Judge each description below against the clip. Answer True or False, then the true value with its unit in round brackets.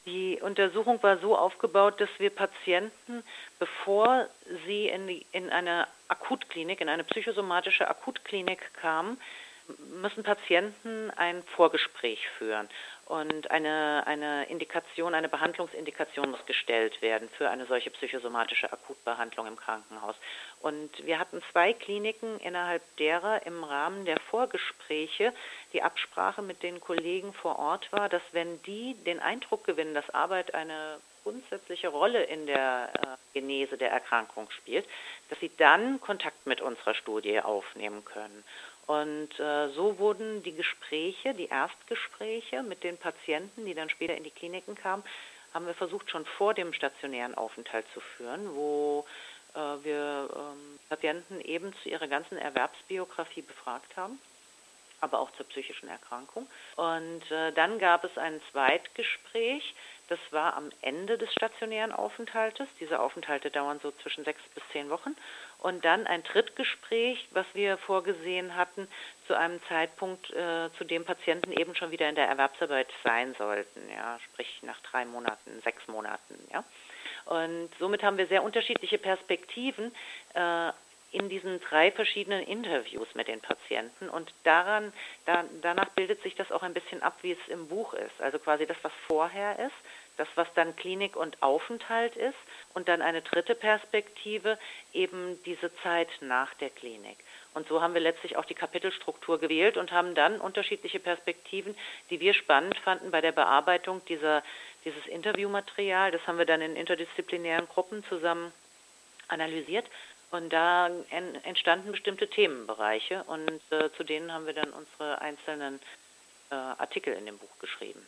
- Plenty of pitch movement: False (4.7 semitones)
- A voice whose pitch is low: False (175 Hz)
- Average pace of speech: True (150 wpm)